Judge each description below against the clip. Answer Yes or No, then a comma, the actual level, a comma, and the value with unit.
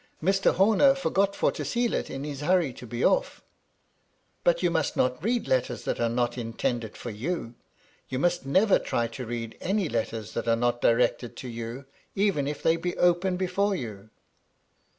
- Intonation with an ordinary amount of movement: No, wide, 7.9 semitones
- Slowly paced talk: No, average, 190 wpm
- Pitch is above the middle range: No, medium, 140 Hz